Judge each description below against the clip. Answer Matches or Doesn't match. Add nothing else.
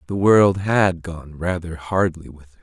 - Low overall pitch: Matches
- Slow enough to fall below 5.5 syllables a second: Matches